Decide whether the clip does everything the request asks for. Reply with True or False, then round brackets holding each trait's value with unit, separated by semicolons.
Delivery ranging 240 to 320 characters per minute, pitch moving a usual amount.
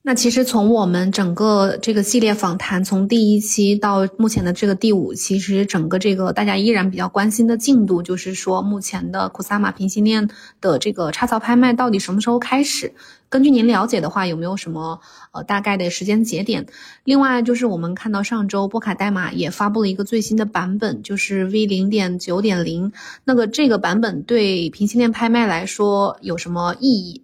True (315 characters per minute; 3.4 semitones)